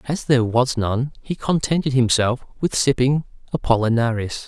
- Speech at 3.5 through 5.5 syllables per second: Yes, 5.0 syllables/s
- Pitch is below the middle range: Yes, low, 125 Hz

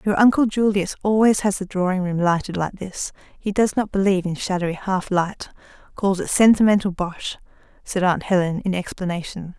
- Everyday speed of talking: Yes, average, 170 wpm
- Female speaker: Yes, female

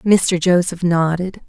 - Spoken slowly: Yes, slow, 120 wpm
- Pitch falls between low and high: Yes, medium, 180 Hz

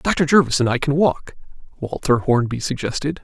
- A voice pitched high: No, medium, 140 Hz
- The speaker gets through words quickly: No, average, 165 wpm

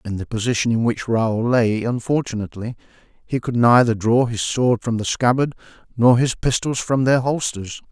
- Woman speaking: No, male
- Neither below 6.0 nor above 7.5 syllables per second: No, 5.0 syllables/s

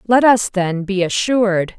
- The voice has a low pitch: No, high, 205 Hz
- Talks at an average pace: Yes, average, 170 wpm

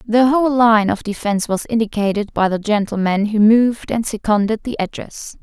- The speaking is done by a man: No, female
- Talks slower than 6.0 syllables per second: Yes, 5.3 syllables/s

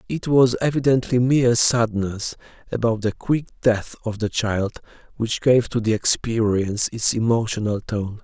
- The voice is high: No, low, 115 Hz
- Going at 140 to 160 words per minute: Yes, average, 145 wpm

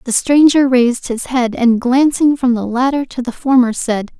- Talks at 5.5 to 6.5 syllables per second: No, 4.7 syllables/s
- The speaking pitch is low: No, very high, 250 Hz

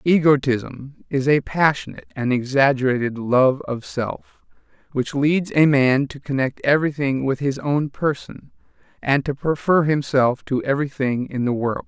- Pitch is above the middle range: No, medium, 140 Hz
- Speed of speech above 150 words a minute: No, average, 145 wpm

